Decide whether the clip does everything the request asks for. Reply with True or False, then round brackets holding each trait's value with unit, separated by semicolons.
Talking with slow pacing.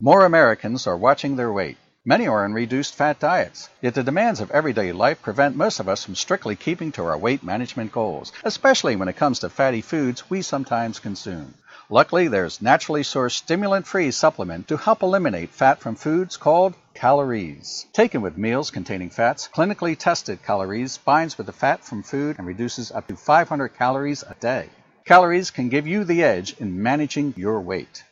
False (180 wpm)